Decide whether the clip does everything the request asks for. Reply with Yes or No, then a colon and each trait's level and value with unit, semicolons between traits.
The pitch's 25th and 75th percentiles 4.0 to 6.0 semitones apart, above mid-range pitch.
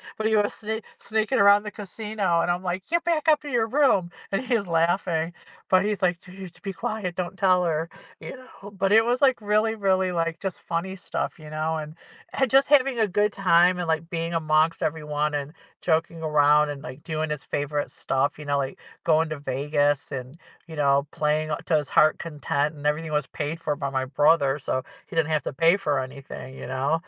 No: average, 5.0 semitones; medium, 165 Hz